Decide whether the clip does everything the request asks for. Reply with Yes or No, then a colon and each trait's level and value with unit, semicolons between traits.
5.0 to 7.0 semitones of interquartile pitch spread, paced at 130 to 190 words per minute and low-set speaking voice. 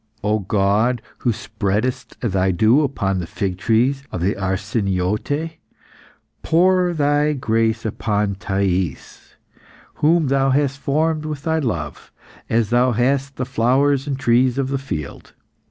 Yes: wide, 5.6 semitones; slow, 135 wpm; low, 120 Hz